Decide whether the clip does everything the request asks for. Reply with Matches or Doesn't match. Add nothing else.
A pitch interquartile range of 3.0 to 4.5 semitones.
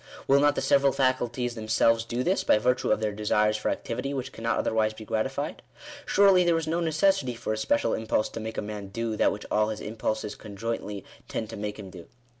Matches